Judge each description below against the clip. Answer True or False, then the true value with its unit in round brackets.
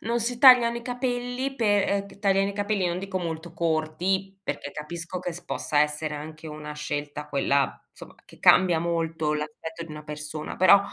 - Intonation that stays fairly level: False (4.7 semitones)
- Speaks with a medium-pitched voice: True (170 Hz)